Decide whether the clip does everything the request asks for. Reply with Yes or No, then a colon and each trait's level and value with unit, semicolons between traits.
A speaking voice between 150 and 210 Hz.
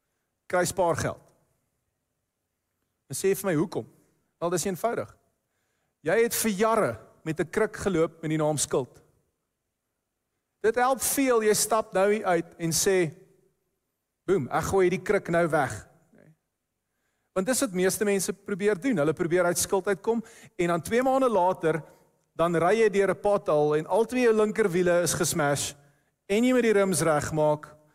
Yes: medium, 185 Hz